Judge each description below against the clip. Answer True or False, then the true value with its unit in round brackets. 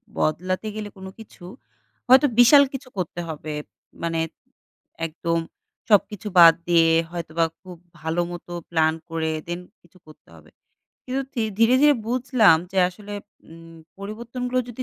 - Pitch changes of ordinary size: False (5.8 semitones)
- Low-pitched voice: False (185 Hz)